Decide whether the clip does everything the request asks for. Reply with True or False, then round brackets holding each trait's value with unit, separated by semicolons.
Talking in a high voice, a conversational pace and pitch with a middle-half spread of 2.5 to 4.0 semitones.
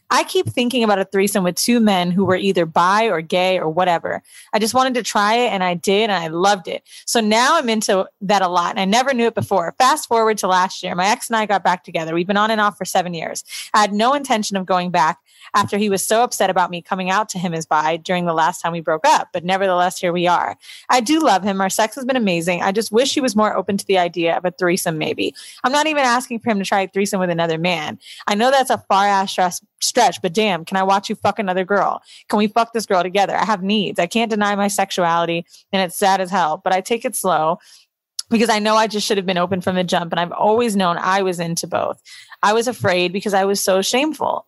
False (195 Hz; 270 wpm; 3.4 semitones)